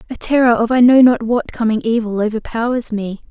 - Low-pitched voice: No, high, 230 Hz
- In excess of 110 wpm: Yes, average, 200 wpm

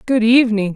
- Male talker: No, female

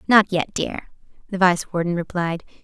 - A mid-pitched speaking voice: Yes, medium, 180 Hz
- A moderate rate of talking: Yes, average, 160 wpm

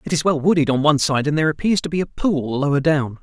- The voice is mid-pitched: Yes, medium, 150 Hz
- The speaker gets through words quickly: Yes, fast, 295 wpm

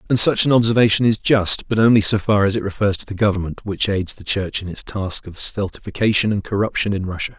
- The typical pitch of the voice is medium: No, low, 100 Hz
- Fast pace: Yes, fast, 235 wpm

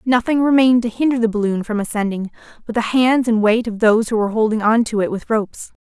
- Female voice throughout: Yes, female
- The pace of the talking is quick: Yes, fast, 235 wpm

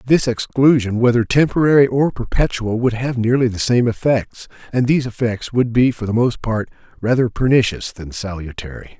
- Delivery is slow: No, average, 165 wpm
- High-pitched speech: No, low, 120 Hz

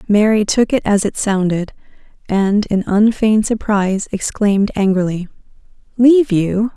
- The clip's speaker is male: No, female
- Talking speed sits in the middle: No, slow, 125 wpm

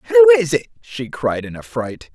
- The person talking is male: Yes, male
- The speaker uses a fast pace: No, average, 195 wpm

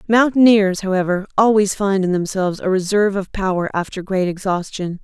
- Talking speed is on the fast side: No, average, 155 wpm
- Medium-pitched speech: No, high, 195 Hz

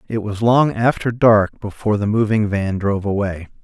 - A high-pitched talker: No, low, 105 Hz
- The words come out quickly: No, average, 180 wpm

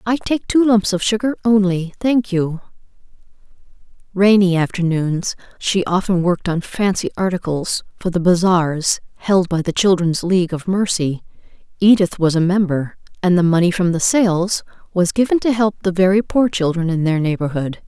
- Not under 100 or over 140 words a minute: No, average, 160 wpm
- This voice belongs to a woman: Yes, female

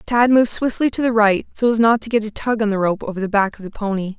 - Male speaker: No, female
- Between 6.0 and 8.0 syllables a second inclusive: Yes, 6.5 syllables/s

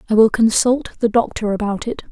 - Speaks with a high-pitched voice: Yes, high, 225 Hz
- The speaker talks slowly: No, average, 200 wpm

